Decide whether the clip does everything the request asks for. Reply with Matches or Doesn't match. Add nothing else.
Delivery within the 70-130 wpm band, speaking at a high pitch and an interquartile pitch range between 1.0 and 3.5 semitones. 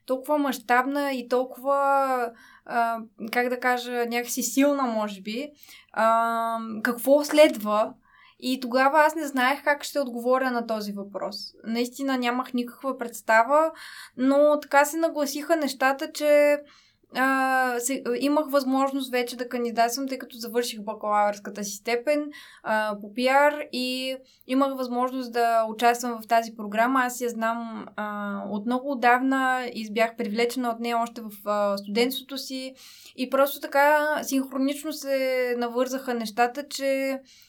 Matches